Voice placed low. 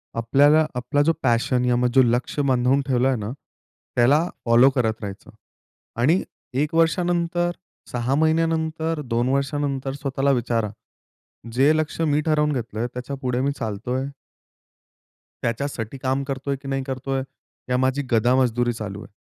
Yes: low, 130 Hz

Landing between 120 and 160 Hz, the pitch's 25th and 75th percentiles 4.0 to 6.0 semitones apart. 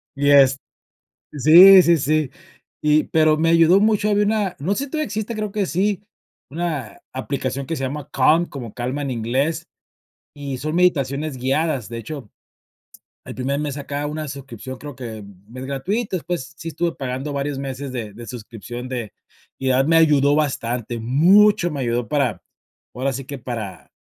Yes: medium, 140 Hz; average, 4.3 semitones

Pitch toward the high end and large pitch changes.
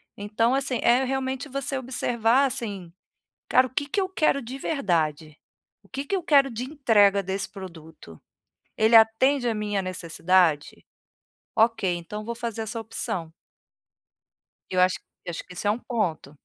Yes: high, 225 Hz; wide, 5.9 semitones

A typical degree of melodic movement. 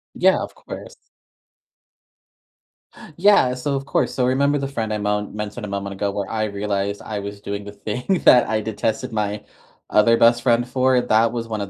Yes: average, 3.4 semitones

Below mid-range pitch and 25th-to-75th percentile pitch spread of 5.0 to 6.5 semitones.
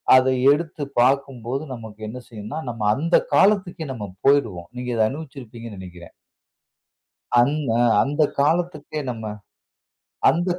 Yes: low, 130 Hz; average, 5.3 semitones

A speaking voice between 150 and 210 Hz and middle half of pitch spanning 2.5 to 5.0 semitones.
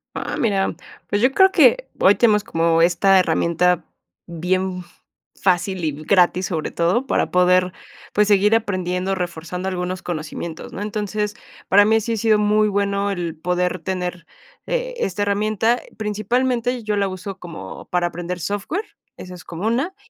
Yes: high, 190 Hz; average, 2.9 semitones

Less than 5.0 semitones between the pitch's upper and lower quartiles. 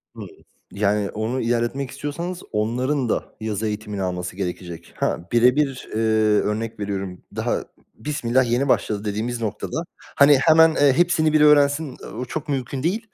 No: wide, 5.4 semitones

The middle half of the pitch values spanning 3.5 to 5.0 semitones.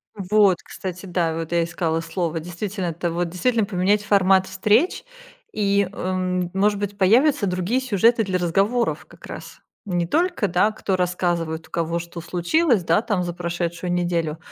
No: average, 3.1 semitones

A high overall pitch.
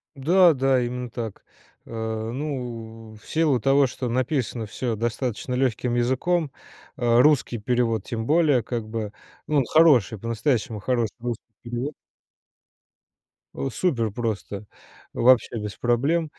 No: low, 120 Hz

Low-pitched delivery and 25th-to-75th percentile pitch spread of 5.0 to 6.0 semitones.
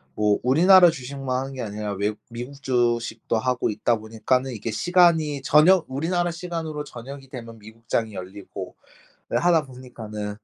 Yes: low, 130 Hz; average, 5.3 semitones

